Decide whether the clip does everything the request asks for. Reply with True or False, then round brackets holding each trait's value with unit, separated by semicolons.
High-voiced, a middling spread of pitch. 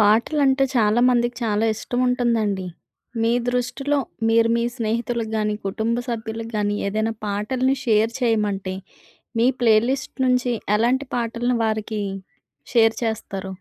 False (230 Hz; 2.3 semitones)